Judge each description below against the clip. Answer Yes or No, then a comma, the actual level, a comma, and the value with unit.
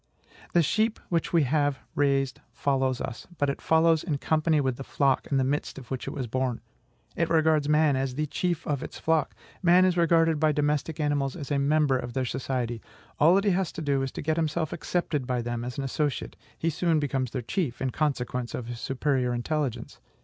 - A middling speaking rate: No, fast, 215 wpm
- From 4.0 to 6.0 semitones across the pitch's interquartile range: No, average, 3.4 semitones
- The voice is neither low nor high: Yes, medium, 145 Hz